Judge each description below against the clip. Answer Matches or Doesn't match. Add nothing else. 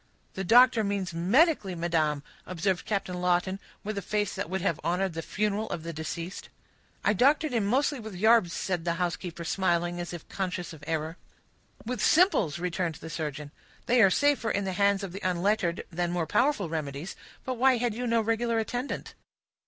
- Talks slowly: Doesn't match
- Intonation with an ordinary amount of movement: Matches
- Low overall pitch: Doesn't match